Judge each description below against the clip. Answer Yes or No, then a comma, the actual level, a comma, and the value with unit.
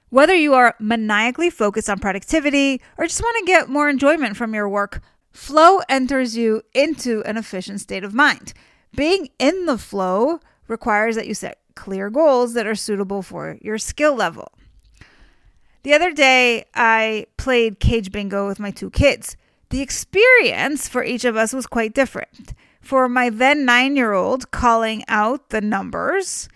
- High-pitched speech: Yes, high, 245 Hz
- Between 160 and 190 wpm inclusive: Yes, average, 165 wpm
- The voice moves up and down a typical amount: Yes, average, 4.8 semitones